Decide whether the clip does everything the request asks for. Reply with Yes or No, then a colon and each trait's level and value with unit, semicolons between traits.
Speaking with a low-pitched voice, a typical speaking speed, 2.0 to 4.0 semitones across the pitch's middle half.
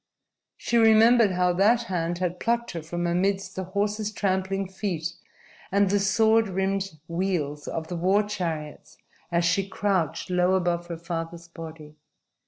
No: medium, 185 Hz; average, 150 wpm; average, 2.9 semitones